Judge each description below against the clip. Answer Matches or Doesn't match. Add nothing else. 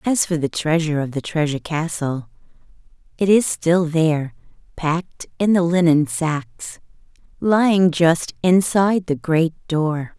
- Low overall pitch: Doesn't match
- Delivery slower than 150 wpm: Matches